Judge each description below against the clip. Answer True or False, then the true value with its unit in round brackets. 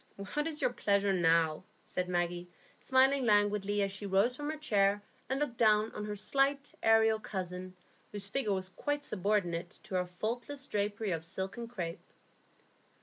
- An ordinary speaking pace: True (165 wpm)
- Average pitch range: True (4.3 semitones)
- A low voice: False (205 Hz)